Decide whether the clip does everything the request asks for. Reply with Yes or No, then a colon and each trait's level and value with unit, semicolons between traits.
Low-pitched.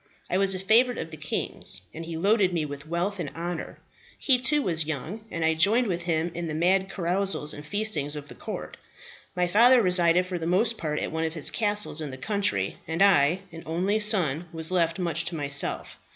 No: medium, 175 Hz